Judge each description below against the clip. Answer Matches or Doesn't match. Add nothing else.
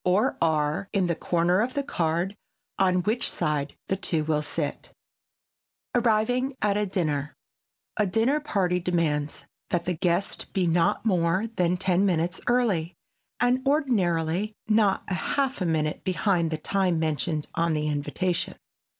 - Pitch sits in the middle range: Matches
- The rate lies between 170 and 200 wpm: Doesn't match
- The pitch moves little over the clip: Doesn't match